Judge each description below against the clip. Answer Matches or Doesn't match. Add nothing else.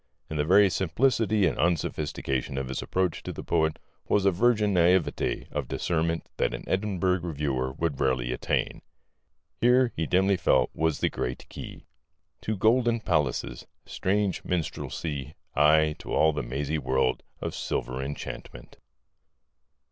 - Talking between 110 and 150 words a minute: Matches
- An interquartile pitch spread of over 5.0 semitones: Matches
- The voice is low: Matches